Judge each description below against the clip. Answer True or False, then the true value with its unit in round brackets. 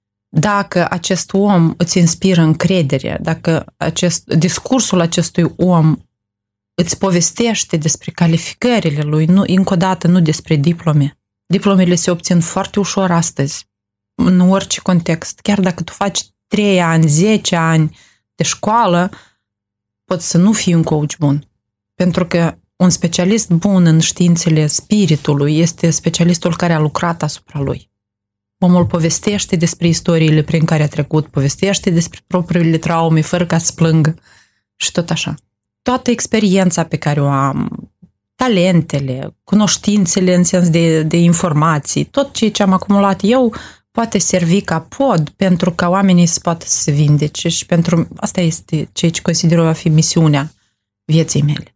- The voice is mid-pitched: True (170 Hz)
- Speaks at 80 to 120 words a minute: False (145 wpm)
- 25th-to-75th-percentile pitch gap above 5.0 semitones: False (3.0 semitones)